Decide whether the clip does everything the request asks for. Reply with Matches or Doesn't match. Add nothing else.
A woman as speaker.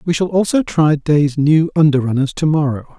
Doesn't match